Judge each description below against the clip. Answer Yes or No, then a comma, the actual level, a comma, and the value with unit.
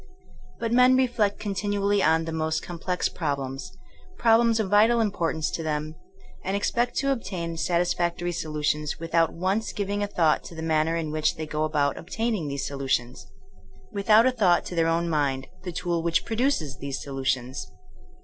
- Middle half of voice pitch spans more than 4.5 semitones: Yes, average, 4.9 semitones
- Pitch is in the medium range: Yes, medium, 170 Hz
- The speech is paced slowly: No, average, 180 wpm